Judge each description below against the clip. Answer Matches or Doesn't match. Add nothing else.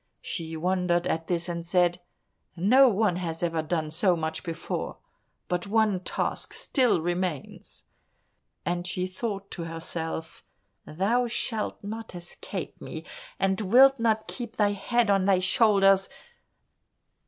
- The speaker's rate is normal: Doesn't match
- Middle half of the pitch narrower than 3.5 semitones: Doesn't match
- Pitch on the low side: Doesn't match